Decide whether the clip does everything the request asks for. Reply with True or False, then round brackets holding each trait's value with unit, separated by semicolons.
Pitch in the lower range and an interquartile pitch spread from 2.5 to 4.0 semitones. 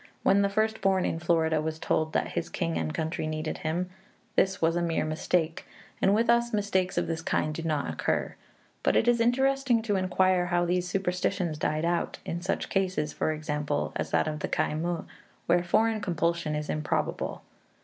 False (175 Hz; 3.7 semitones)